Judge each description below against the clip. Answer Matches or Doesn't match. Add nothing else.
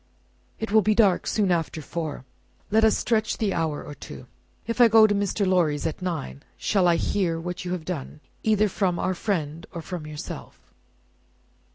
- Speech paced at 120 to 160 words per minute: Doesn't match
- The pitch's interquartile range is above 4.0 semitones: Matches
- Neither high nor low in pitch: Matches